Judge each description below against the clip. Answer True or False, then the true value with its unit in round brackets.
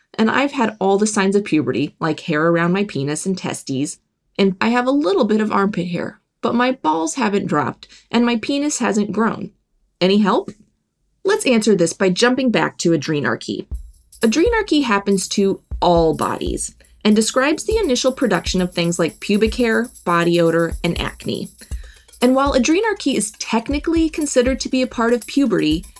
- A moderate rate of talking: True (175 wpm)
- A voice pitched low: False (210 Hz)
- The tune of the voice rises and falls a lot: True (6.6 semitones)